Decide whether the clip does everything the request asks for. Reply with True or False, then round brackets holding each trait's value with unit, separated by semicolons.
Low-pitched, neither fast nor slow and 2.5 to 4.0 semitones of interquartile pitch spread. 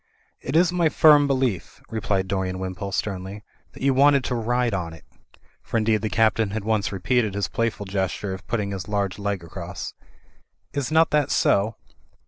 False (105 Hz; 180 wpm; 4.6 semitones)